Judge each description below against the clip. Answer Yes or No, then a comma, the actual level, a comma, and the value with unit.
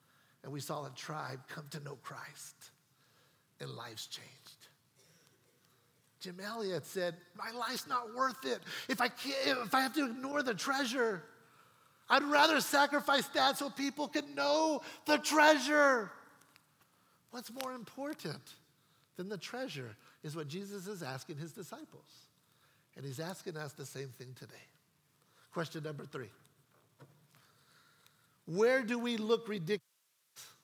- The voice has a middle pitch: Yes, medium, 170 Hz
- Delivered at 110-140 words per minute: Yes, slow, 135 wpm